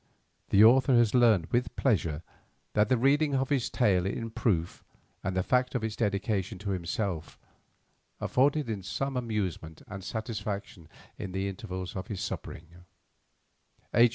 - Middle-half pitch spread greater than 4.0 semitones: Yes, average, 4.6 semitones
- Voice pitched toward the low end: Yes, low, 105 Hz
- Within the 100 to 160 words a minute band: Yes, average, 150 wpm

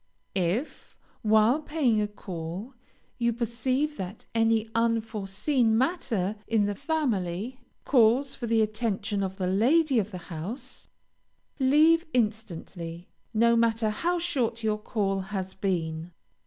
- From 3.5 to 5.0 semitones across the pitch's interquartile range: Yes, average, 4.5 semitones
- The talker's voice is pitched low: No, high, 220 Hz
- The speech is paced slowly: Yes, slow, 125 wpm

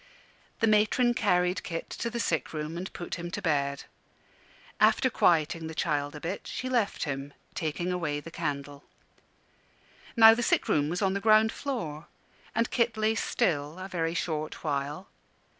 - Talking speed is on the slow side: No, average, 165 wpm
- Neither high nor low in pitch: Yes, medium, 175 Hz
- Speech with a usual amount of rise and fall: No, wide, 6.2 semitones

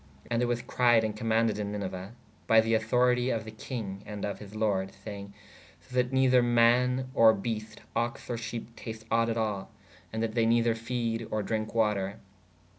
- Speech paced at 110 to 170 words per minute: No, average, 190 wpm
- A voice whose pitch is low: Yes, low, 115 Hz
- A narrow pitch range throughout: Yes, narrow, 2.0 semitones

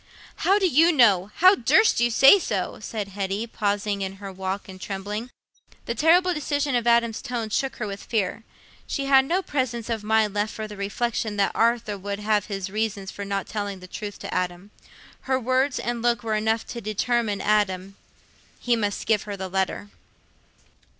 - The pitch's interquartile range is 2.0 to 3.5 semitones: Yes, average, 3.2 semitones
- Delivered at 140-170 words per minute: No, average, 185 wpm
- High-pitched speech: Yes, high, 215 Hz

